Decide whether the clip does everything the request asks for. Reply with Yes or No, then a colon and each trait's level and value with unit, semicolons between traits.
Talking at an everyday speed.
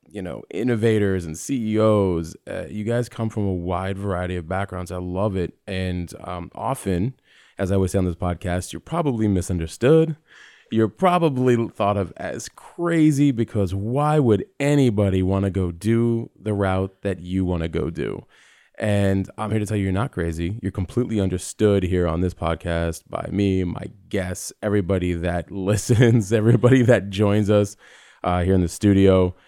Yes: average, 175 wpm